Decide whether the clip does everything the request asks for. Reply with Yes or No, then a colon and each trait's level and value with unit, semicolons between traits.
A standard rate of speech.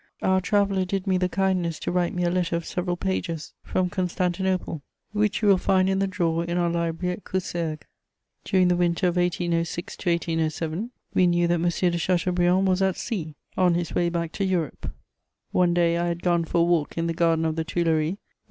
No: fast, 215 wpm